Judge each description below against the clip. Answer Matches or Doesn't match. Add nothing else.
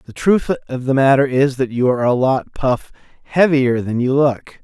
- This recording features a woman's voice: Doesn't match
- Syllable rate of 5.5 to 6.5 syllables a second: Doesn't match